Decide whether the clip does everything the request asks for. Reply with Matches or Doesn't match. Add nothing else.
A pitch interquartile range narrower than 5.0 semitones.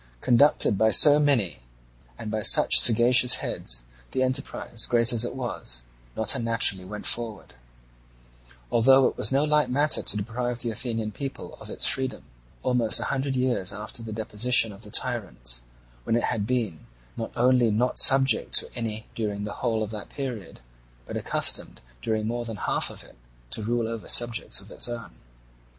Matches